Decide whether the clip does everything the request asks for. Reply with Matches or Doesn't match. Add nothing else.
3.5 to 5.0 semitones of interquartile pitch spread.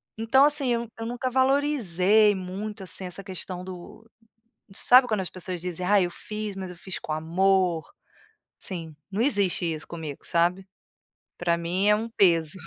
Matches